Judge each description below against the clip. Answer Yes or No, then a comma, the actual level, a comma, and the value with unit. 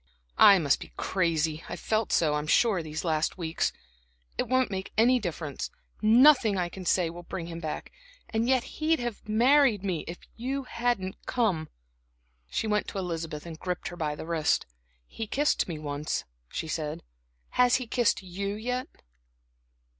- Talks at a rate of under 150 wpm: No, average, 165 wpm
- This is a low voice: No, high, 190 Hz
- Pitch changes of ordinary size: No, wide, 6.3 semitones